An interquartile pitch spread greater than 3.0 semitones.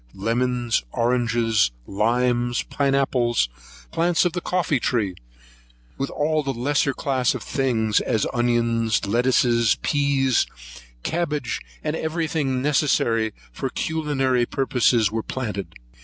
Yes: average, 3.4 semitones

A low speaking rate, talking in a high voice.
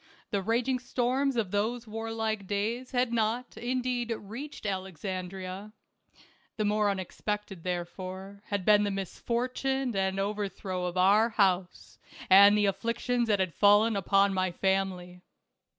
Yes: slow, 130 wpm; high, 205 Hz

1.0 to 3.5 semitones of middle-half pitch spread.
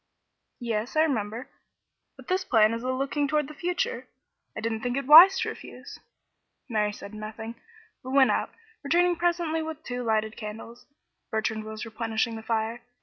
No: wide, 5.6 semitones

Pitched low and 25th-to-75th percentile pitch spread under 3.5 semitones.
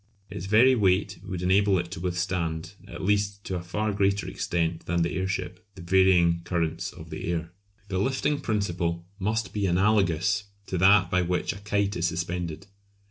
Yes: very low, 95 Hz; narrow, 2.6 semitones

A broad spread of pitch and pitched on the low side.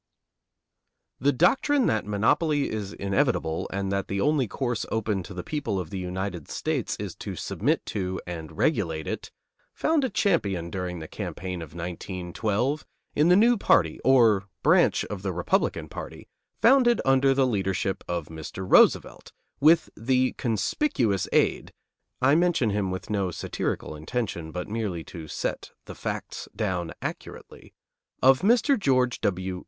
Yes: wide, 6.7 semitones; low, 105 Hz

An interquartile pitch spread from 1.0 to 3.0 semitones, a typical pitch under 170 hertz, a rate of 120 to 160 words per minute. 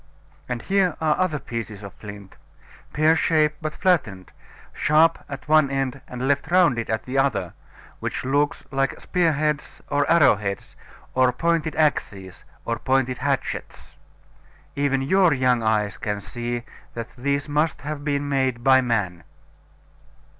No: average, 4.6 semitones; low, 135 Hz; average, 145 wpm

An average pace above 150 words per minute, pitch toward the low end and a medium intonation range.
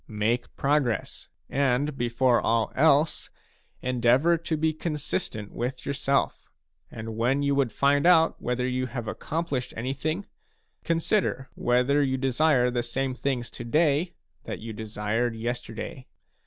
No: slow, 135 wpm; low, 130 Hz; average, 3.5 semitones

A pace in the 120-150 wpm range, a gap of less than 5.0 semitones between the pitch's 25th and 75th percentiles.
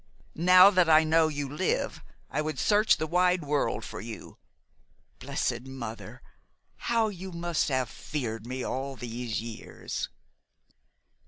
No: slow, 135 wpm; wide, 5.6 semitones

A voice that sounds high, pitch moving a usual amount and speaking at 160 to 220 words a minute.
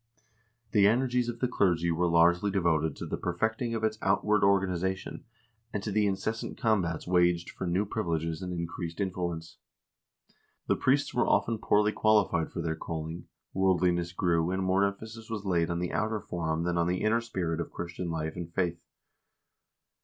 No: very low, 90 Hz; average, 3.8 semitones; average, 170 wpm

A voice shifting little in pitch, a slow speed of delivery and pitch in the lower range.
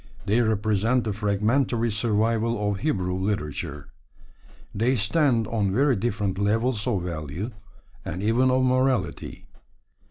No: average, 3.3 semitones; slow, 120 wpm; low, 110 Hz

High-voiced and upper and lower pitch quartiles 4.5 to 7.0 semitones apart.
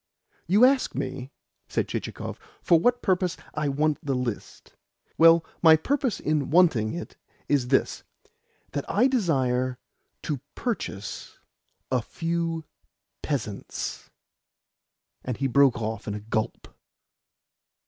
No: medium, 145 Hz; average, 5.2 semitones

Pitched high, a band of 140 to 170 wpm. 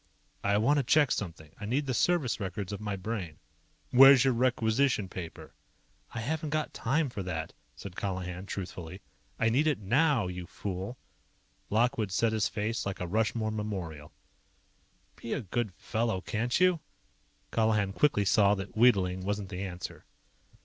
No: low, 105 Hz; average, 155 wpm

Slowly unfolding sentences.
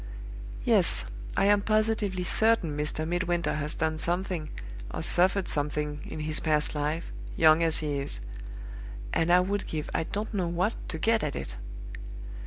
No: average, 160 wpm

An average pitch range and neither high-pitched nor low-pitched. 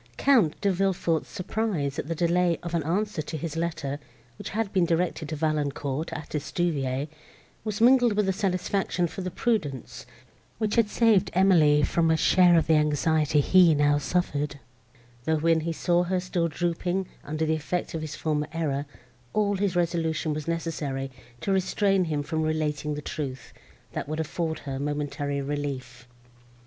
Yes: average, 3.6 semitones; medium, 160 Hz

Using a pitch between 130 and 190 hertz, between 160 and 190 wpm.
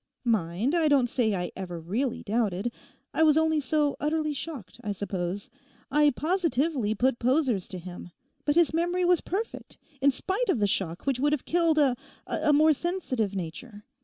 No: very high, 265 Hz; average, 170 wpm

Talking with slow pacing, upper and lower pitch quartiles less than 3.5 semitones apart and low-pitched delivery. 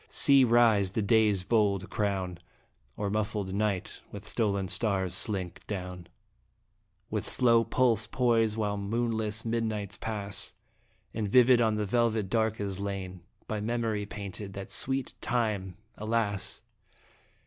Yes: slow, 125 wpm; narrow, 2.4 semitones; low, 105 Hz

